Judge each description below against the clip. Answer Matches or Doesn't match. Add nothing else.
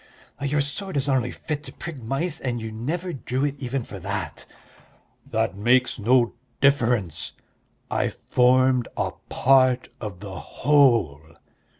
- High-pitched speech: Doesn't match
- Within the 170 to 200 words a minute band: Doesn't match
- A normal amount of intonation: Matches